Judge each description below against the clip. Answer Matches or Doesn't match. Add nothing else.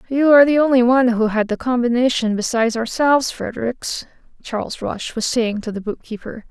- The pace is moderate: Matches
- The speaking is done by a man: Doesn't match